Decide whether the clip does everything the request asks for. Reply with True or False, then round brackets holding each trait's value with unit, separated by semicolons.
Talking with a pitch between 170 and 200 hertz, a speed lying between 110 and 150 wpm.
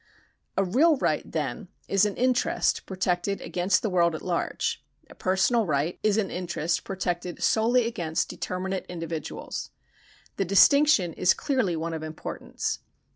True (185 Hz; 140 wpm)